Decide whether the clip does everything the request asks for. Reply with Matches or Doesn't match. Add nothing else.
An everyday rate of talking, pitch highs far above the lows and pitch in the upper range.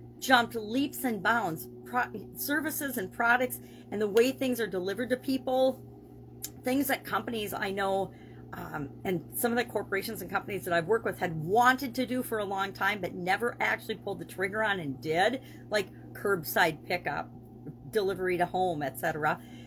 Matches